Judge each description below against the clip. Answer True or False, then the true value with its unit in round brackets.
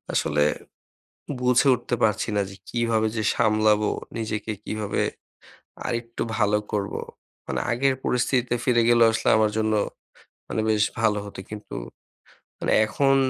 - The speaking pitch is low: True (110 Hz)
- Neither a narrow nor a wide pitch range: False (1.9 semitones)